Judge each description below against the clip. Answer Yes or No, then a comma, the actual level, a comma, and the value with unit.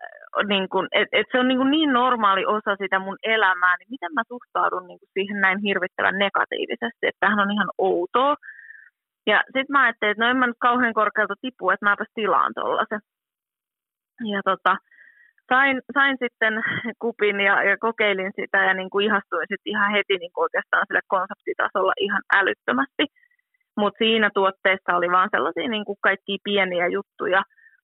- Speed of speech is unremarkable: No, fast, 170 wpm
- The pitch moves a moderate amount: Yes, average, 4.0 semitones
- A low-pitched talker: No, high, 205 Hz